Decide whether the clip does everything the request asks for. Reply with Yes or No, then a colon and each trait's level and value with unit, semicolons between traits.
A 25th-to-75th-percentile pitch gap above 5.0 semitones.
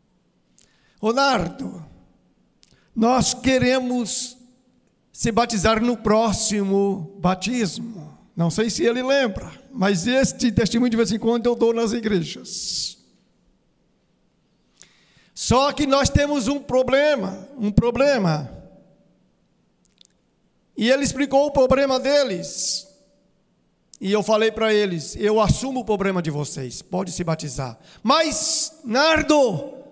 Yes: wide, 5.4 semitones